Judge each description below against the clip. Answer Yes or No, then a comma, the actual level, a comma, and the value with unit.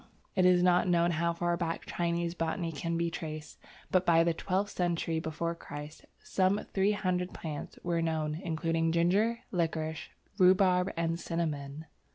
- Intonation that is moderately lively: No, narrow, 1.9 semitones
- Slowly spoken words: No, average, 155 wpm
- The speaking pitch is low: No, medium, 170 Hz